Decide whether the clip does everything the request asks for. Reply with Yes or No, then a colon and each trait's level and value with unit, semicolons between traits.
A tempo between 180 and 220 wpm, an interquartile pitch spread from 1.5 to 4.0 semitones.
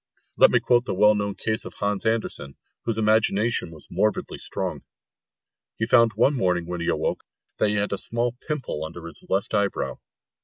Yes: average, 185 wpm; average, 3.3 semitones